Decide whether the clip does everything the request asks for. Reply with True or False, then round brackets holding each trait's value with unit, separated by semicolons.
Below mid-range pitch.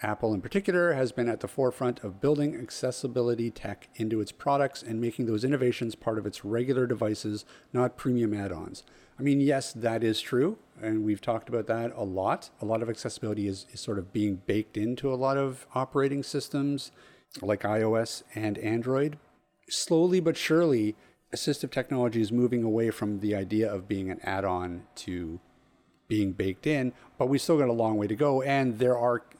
True (115 Hz)